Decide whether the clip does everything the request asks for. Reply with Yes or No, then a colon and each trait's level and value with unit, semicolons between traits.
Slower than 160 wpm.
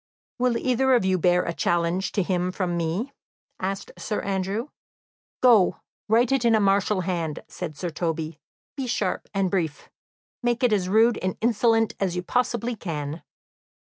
No: average, 165 wpm